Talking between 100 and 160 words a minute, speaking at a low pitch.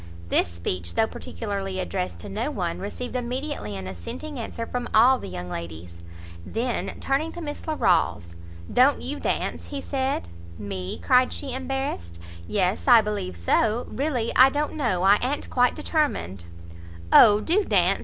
No: average, 155 wpm; high, 230 Hz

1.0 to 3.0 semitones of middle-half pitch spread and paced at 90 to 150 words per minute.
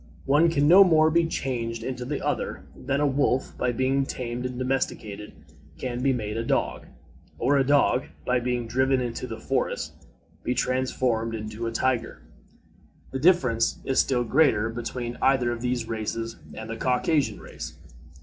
No: average, 2.7 semitones; average, 165 wpm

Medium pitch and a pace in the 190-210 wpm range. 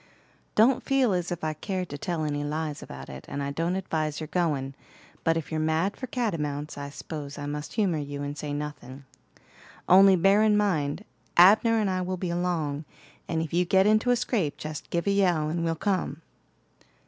Yes: medium, 165 Hz; average, 200 wpm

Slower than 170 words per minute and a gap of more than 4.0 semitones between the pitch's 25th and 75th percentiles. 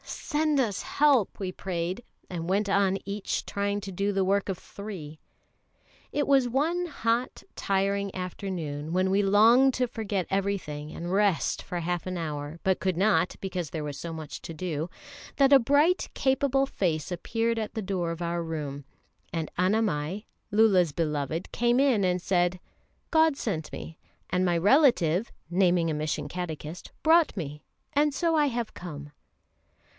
Yes: average, 160 wpm; average, 5.3 semitones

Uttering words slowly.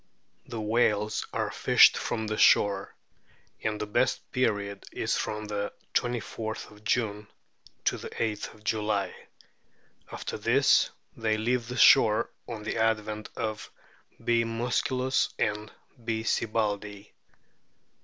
Yes: slow, 115 wpm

